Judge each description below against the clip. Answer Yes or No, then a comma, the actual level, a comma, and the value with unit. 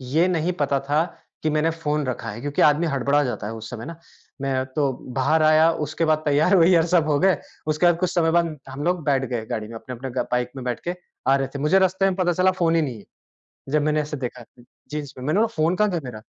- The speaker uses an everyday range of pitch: Yes, average, 4.0 semitones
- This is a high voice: No, medium, 150 Hz